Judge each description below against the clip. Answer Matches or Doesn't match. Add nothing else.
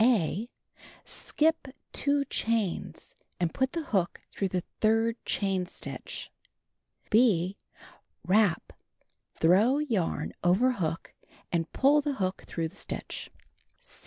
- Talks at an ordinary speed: Doesn't match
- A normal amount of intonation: Doesn't match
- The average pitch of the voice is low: Doesn't match